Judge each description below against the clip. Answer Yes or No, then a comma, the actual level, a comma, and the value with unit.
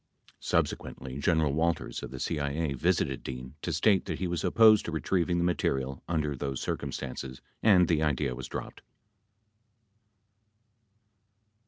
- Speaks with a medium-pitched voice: No, very low, 75 Hz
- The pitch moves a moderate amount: Yes, average, 4.3 semitones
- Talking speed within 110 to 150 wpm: Yes, average, 140 wpm